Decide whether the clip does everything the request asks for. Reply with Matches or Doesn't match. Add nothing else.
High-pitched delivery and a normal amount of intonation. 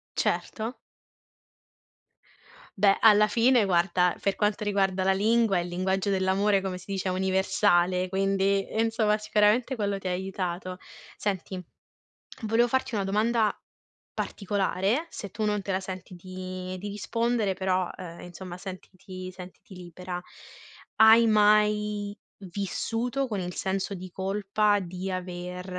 Doesn't match